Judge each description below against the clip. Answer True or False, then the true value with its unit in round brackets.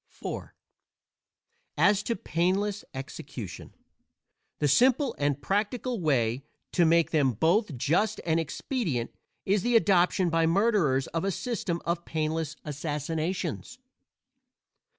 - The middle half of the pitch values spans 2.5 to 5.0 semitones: False (5.4 semitones)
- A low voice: False (170 Hz)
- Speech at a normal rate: False (110 wpm)